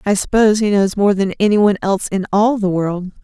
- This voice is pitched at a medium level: No, high, 200 Hz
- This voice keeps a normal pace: No, fast, 225 wpm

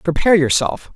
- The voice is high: No, medium, 170 Hz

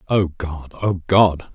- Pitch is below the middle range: Yes, very low, 90 Hz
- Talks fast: No, average, 155 wpm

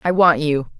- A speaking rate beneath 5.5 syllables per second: Yes, 4.7 syllables/s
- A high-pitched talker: No, medium, 155 Hz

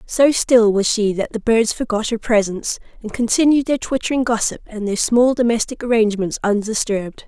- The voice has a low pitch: No, high, 225 Hz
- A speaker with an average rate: Yes, average, 175 wpm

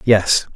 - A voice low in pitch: Yes, low, 105 Hz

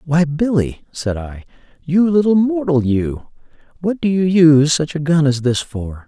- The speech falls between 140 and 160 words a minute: No, average, 180 wpm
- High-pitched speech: No, medium, 155 Hz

